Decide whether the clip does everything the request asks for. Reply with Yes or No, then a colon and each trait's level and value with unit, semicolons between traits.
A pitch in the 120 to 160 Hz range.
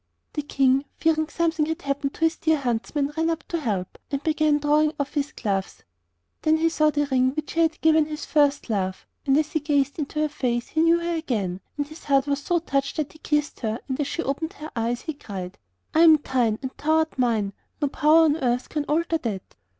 No: very high, 295 Hz